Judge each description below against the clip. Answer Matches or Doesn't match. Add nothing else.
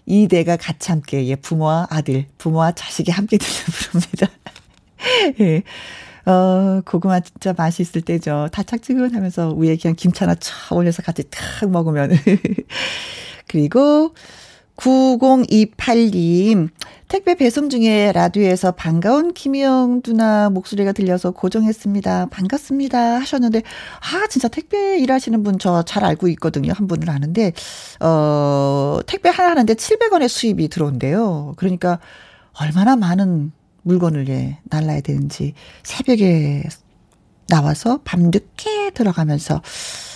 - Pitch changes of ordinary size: Doesn't match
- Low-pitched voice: Doesn't match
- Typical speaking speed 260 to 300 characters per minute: Matches